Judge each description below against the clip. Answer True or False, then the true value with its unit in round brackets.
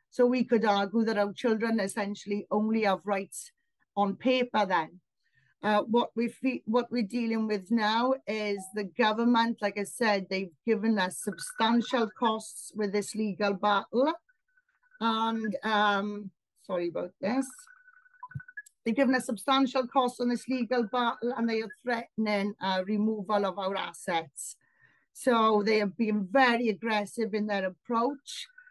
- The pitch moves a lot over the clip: False (3.3 semitones)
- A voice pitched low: False (225 Hz)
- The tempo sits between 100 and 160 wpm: True (145 wpm)